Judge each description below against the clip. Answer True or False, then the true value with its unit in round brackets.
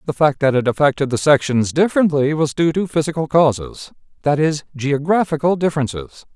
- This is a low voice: False (150 Hz)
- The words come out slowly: False (150 wpm)